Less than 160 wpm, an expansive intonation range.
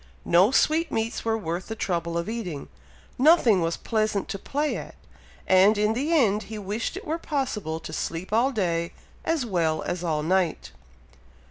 No: average, 165 wpm; wide, 5.9 semitones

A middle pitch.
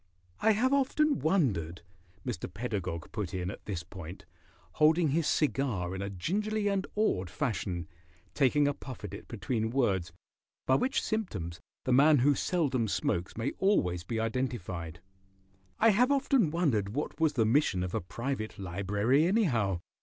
No: low, 120 Hz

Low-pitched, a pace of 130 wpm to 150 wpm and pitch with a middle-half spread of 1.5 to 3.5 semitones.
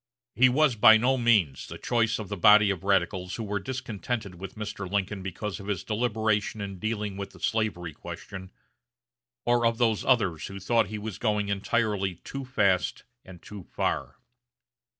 No: low, 105 Hz; average, 170 wpm; average, 3.0 semitones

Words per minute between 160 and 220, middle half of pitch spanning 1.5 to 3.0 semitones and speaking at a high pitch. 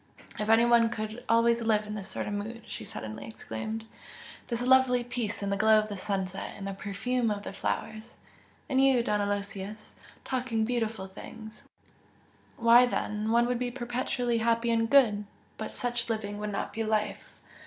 Yes: average, 175 wpm; narrow, 2.4 semitones; high, 225 Hz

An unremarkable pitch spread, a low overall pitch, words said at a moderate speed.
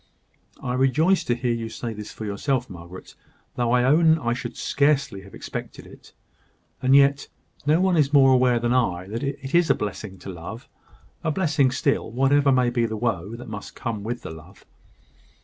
Yes: average, 4.3 semitones; low, 125 Hz; average, 190 wpm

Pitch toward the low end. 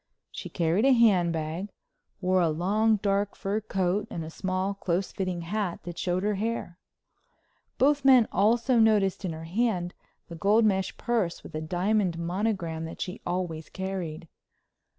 No: high, 190 Hz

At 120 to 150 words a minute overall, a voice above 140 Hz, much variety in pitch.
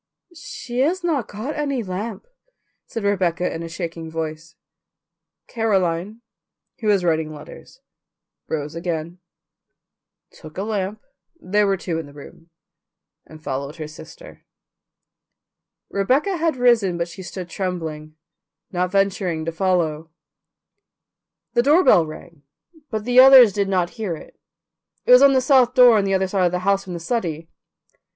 Yes: average, 145 wpm; medium, 185 Hz; wide, 5.8 semitones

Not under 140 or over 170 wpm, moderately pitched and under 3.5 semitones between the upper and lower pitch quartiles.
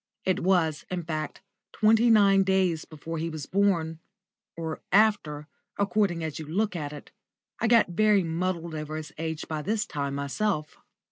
No: average, 160 wpm; medium, 170 Hz; average, 4.3 semitones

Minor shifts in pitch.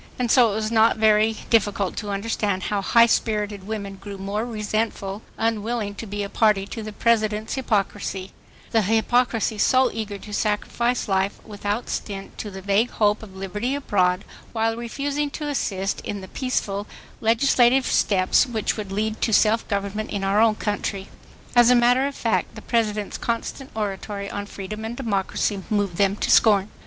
Yes: narrow, 2.3 semitones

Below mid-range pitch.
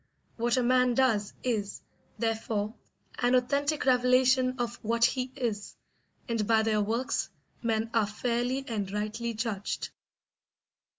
No: high, 235 Hz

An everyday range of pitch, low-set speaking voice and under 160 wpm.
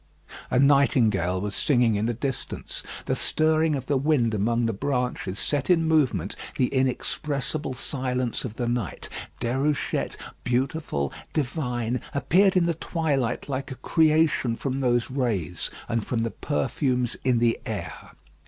Yes: average, 3.7 semitones; low, 130 Hz; average, 145 wpm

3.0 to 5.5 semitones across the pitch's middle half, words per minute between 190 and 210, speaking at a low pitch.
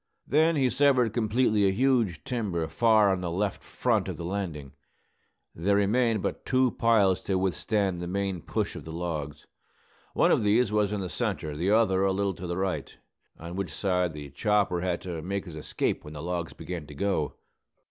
Yes: average, 3.7 semitones; average, 195 wpm; very low, 95 Hz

